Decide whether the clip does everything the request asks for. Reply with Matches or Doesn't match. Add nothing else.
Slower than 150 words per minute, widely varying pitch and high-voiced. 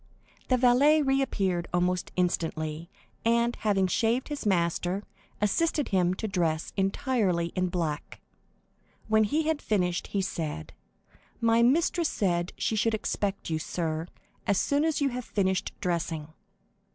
Matches